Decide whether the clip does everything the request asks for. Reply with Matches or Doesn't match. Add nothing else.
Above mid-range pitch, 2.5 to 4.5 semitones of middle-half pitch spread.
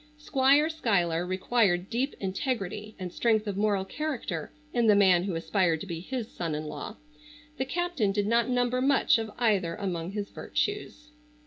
Doesn't match